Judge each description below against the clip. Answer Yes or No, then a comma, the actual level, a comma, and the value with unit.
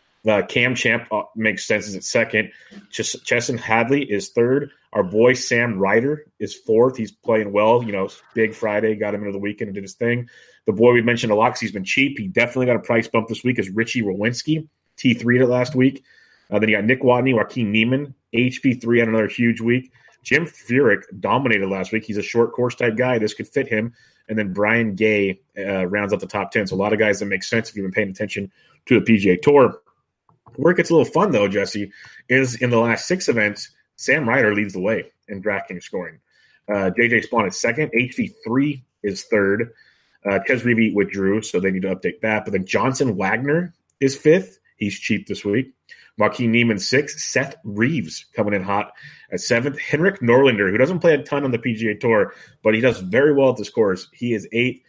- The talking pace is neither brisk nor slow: No, fast, 215 wpm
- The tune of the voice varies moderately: Yes, average, 3.2 semitones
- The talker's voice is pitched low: Yes, low, 115 Hz